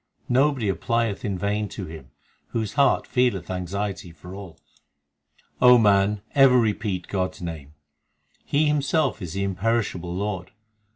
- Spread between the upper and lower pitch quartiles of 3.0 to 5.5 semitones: Yes, average, 4.3 semitones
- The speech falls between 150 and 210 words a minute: No, slow, 135 wpm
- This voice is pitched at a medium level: No, low, 100 Hz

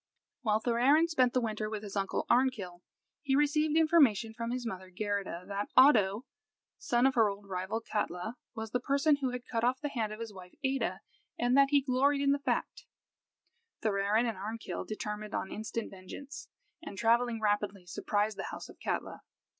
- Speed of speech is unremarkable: Yes, average, 180 wpm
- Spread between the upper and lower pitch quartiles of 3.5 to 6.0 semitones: Yes, average, 4.3 semitones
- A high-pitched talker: Yes, high, 230 Hz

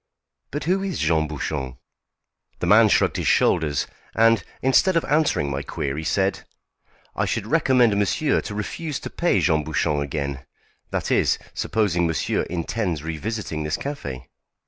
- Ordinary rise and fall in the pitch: No, wide, 7.6 semitones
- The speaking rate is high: No, average, 145 wpm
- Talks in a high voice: No, very low, 90 Hz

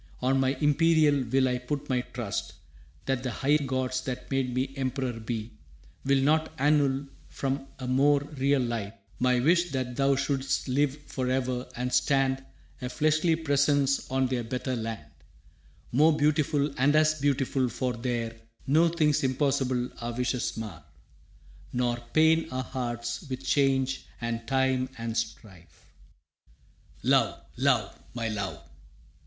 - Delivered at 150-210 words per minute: No, average, 140 wpm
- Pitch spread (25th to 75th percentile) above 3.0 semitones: No, narrow, 2.4 semitones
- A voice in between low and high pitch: No, low, 130 Hz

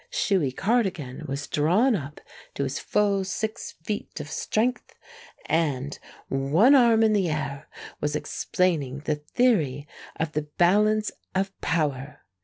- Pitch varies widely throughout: Yes, wide, 6.5 semitones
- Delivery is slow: Yes, slow, 130 wpm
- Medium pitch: Yes, medium, 165 Hz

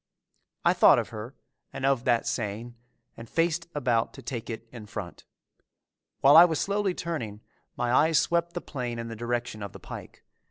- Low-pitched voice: Yes, low, 120 Hz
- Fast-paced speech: No, average, 185 wpm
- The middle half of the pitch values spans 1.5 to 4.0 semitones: No, wide, 5.6 semitones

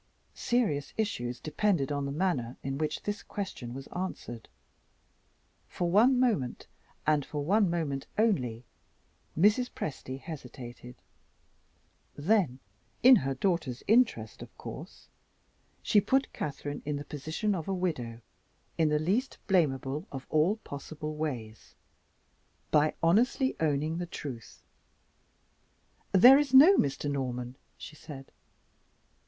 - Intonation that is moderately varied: No, wide, 6.6 semitones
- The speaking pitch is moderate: Yes, medium, 155 Hz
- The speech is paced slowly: Yes, slow, 120 wpm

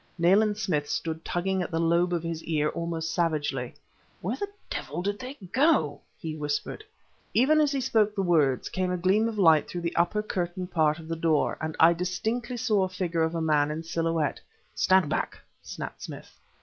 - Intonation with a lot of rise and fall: No, average, 3.8 semitones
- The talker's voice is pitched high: No, medium, 170 Hz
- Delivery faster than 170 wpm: Yes, average, 195 wpm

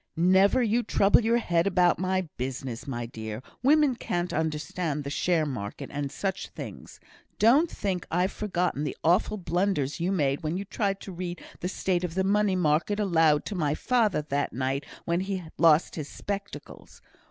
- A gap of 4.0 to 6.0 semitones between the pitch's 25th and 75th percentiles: Yes, average, 4.7 semitones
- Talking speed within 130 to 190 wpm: Yes, average, 175 wpm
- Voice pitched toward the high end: No, medium, 175 Hz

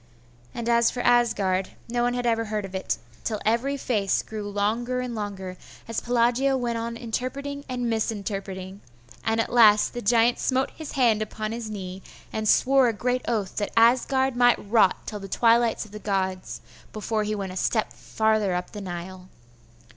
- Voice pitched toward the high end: Yes, high, 225 Hz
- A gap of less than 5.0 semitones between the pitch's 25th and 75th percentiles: Yes, average, 3.0 semitones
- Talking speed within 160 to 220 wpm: Yes, average, 180 wpm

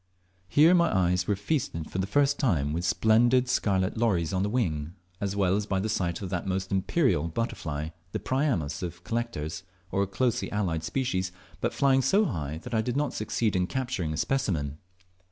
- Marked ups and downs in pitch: Yes, wide, 5.9 semitones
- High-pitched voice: No, low, 100 Hz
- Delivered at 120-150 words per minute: No, average, 190 wpm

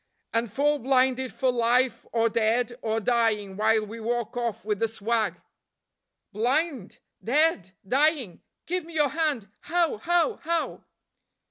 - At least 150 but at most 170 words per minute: No, slow, 135 wpm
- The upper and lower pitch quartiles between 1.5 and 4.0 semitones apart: No, average, 4.9 semitones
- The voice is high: Yes, high, 240 Hz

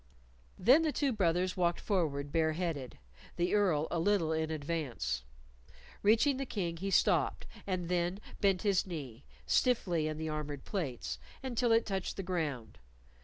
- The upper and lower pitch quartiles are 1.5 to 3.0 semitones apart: No, average, 4.4 semitones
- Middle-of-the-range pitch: Yes, medium, 175 Hz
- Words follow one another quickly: No, average, 155 wpm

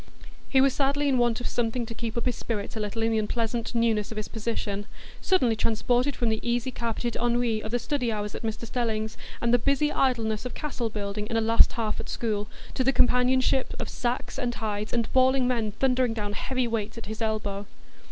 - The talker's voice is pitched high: Yes, high, 230 Hz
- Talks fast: Yes, fast, 210 wpm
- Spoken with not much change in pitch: Yes, narrow, 2.3 semitones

